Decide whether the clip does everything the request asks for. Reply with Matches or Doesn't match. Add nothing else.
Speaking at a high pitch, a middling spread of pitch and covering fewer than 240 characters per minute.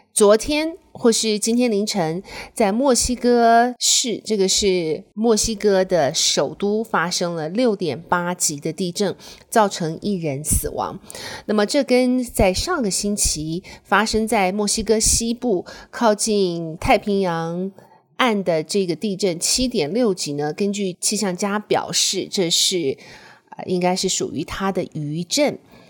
Matches